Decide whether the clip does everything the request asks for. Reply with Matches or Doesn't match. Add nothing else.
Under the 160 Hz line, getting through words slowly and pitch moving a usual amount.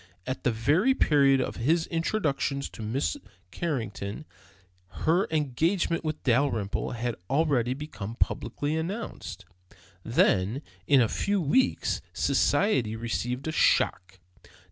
Doesn't match